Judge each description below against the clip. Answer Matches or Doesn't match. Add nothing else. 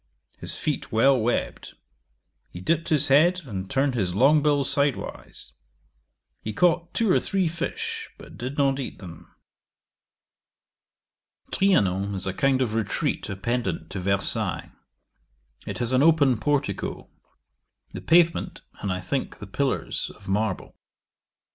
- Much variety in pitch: Matches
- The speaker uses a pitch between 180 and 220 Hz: Doesn't match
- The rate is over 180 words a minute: Doesn't match